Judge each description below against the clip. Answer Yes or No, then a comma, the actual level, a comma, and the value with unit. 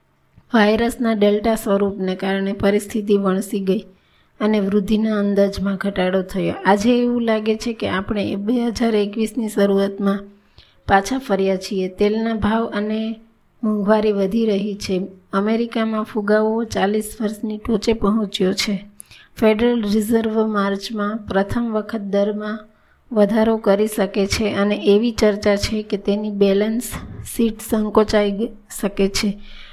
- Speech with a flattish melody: Yes, narrow, 1.8 semitones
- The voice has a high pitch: Yes, high, 210 Hz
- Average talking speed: Yes, average, 120 wpm